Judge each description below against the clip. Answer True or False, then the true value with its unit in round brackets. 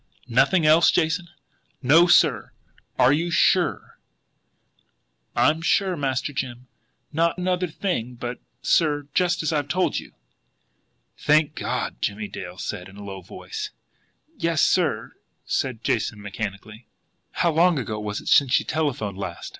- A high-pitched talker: False (145 Hz)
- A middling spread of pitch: False (7.2 semitones)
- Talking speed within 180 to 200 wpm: False (140 wpm)